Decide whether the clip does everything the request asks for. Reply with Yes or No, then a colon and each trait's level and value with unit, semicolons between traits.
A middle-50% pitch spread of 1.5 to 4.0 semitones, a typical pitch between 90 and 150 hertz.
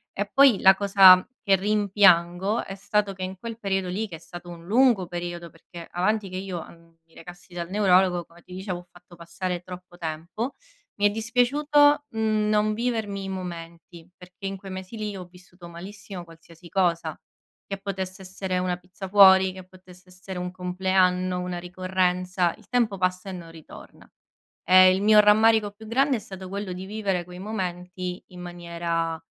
No: narrow, 2.4 semitones; medium, 185 Hz